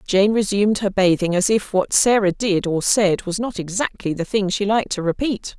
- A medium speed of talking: No, fast, 215 wpm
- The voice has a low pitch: No, high, 200 Hz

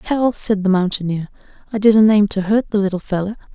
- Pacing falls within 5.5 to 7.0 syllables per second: Yes, 5.6 syllables/s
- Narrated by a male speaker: No, female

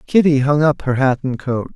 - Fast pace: Yes, fast, 240 wpm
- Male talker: Yes, male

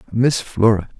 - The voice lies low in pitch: Yes, low, 110 Hz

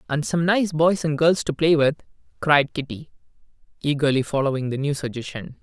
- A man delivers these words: Yes, male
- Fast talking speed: No, average, 170 wpm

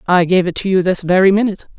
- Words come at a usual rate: No, fast, 270 wpm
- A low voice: No, medium, 185 Hz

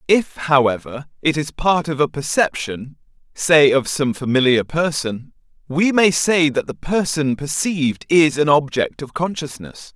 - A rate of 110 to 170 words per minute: Yes, average, 150 wpm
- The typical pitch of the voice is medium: Yes, medium, 150 Hz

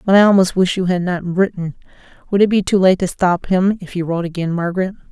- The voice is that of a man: No, female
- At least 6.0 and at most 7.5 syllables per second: Yes, 6.3 syllables/s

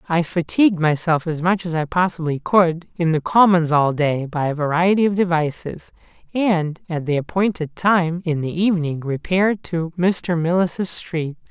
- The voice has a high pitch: No, medium, 170 Hz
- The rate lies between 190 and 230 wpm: No, average, 165 wpm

